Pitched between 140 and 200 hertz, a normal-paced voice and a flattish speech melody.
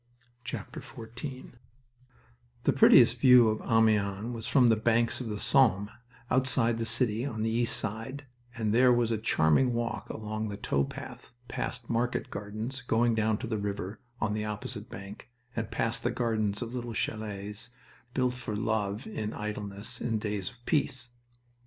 No: low, 115 Hz; average, 160 wpm; narrow, 2.3 semitones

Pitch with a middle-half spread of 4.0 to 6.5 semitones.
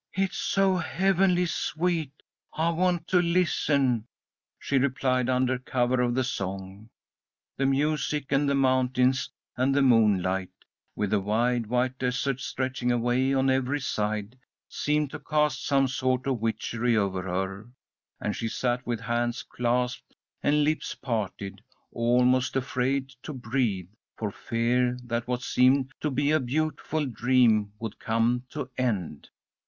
No: average, 3.0 semitones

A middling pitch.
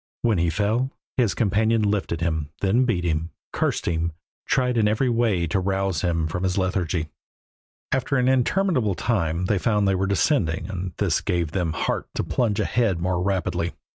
No: very low, 95 Hz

